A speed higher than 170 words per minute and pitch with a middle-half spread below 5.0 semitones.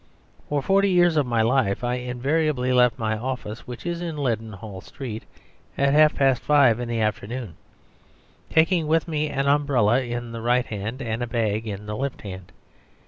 Yes: average, 180 wpm; average, 4.4 semitones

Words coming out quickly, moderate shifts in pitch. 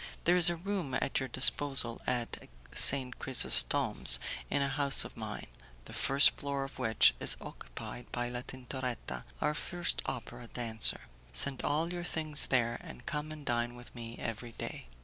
No: average, 170 wpm; average, 3.5 semitones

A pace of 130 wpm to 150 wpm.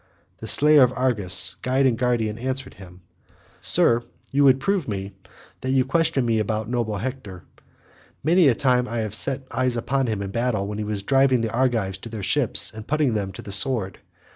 No: average, 195 wpm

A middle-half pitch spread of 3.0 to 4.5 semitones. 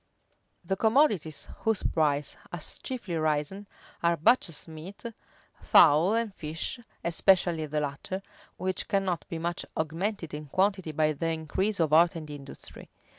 Yes: average, 3.9 semitones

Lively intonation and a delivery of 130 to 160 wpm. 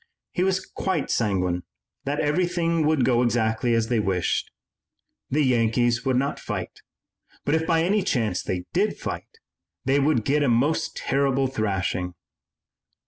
Yes: wide, 5.8 semitones; average, 145 wpm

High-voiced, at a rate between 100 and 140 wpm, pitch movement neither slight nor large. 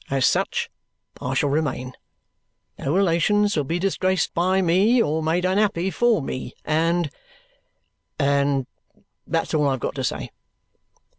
No: medium, 165 Hz; slow, 135 wpm; average, 4.8 semitones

